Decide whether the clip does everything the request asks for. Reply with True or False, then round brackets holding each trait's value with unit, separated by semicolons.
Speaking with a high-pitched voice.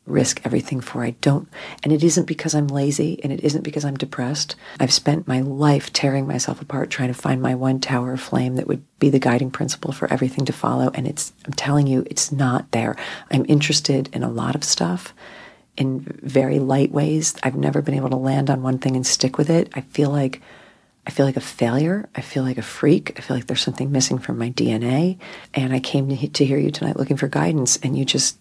False (140 Hz)